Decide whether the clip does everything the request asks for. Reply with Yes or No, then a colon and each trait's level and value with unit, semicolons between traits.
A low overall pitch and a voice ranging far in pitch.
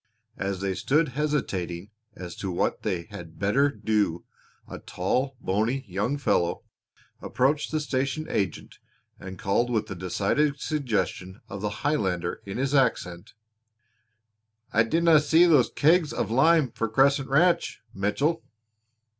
Yes: low, 120 Hz; wide, 7.1 semitones